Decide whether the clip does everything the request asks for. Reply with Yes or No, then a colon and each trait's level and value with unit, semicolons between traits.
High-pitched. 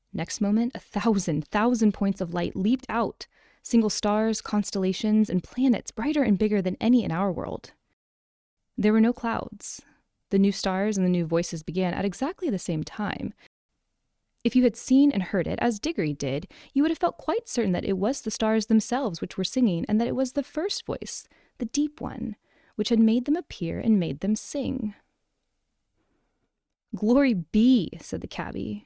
Yes: high, 215 Hz